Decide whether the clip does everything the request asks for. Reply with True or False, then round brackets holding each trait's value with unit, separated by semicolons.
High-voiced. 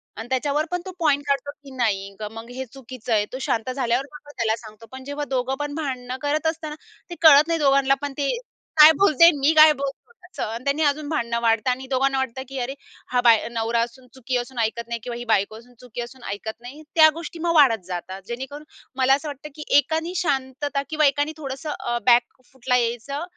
True (265 Hz)